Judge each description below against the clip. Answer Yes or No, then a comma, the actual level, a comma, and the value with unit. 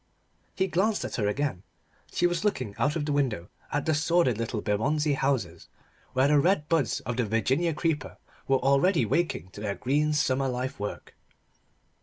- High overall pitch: No, medium, 140 Hz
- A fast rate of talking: No, average, 175 wpm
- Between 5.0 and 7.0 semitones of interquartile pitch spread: Yes, average, 5.3 semitones